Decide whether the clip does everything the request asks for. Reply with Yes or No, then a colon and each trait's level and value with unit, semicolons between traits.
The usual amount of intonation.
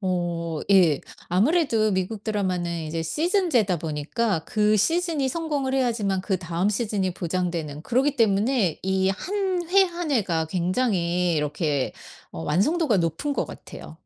No: wide, 7.4 semitones